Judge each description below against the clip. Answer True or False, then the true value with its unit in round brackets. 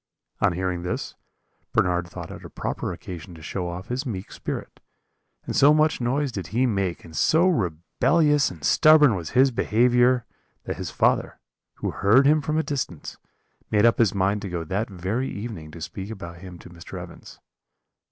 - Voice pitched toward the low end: True (100 Hz)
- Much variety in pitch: True (6.6 semitones)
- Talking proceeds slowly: False (180 wpm)